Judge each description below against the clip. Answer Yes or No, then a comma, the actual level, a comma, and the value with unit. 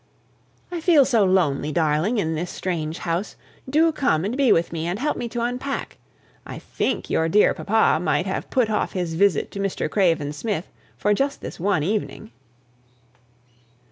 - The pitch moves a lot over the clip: Yes, wide, 6.5 semitones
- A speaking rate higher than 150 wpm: Yes, average, 170 wpm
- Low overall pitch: No, high, 195 Hz